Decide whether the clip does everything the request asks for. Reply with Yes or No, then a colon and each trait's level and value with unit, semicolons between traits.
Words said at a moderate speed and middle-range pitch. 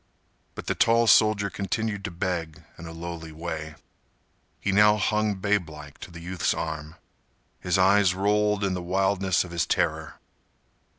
No: average, 155 wpm; very low, 95 Hz